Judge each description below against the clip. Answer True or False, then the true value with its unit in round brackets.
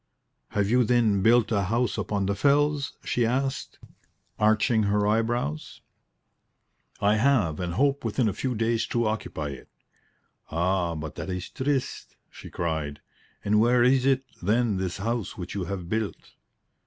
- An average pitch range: True (4.4 semitones)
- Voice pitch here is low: True (110 Hz)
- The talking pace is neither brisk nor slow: True (155 wpm)